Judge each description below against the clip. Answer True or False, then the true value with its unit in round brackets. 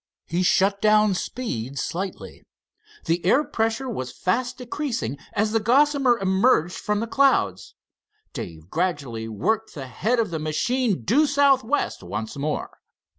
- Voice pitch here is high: True (205 Hz)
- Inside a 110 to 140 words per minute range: True (135 wpm)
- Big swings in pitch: True (8.6 semitones)